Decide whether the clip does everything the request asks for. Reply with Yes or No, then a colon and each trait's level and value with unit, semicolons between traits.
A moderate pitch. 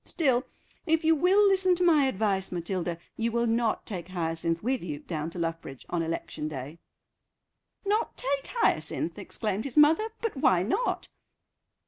No: high, 225 Hz